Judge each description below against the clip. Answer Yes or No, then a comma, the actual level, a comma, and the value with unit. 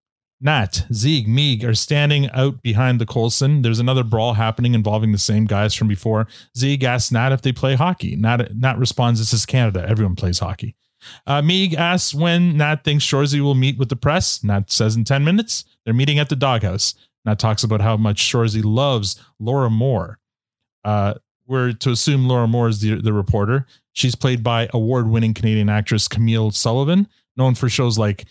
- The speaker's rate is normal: Yes, average, 185 wpm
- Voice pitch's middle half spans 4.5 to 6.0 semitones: No, average, 3.4 semitones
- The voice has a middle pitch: No, low, 120 Hz